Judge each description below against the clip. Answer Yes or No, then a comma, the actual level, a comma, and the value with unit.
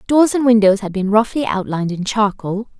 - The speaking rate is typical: Yes, average, 195 wpm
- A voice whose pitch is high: Yes, high, 215 Hz